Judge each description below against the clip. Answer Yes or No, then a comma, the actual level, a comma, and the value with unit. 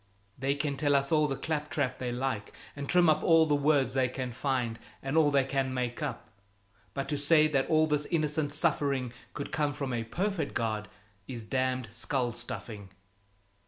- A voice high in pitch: No, medium, 140 Hz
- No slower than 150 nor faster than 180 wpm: No, average, 190 wpm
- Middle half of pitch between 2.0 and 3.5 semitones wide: Yes, average, 2.9 semitones